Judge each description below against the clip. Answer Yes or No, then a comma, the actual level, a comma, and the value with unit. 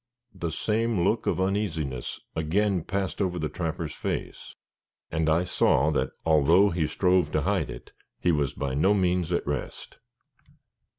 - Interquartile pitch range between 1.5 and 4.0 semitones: Yes, average, 3.7 semitones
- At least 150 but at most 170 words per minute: Yes, average, 155 wpm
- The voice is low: Yes, very low, 90 Hz